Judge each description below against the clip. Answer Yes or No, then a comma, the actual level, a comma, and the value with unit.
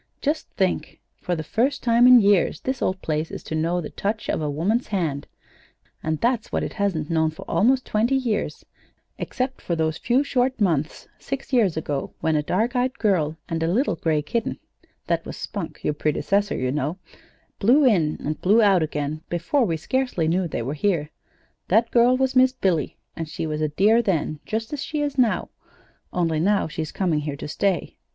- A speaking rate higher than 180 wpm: Yes, average, 195 wpm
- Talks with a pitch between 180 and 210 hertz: Yes, medium, 185 Hz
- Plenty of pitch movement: Yes, wide, 7.1 semitones